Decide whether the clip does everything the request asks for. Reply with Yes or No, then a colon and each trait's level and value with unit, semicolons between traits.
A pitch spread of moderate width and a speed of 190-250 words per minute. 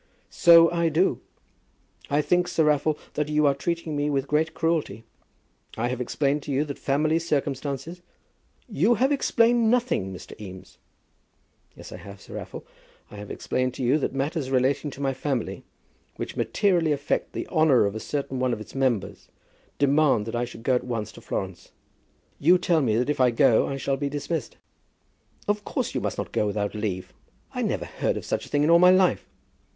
Yes: average, 4.6 semitones; average, 195 wpm